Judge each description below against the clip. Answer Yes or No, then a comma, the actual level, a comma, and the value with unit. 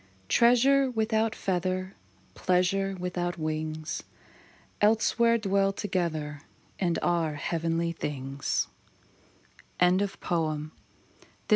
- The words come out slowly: Yes, slow, 85 wpm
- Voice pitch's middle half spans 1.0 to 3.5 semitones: No, average, 4.1 semitones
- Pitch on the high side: No, medium, 180 Hz